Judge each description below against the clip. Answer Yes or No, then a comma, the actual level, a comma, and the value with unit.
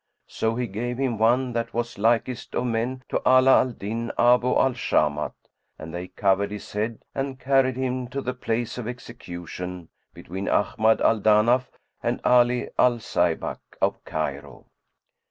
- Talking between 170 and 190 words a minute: No, average, 155 wpm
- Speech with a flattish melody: No, average, 3.7 semitones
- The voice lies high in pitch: No, low, 115 Hz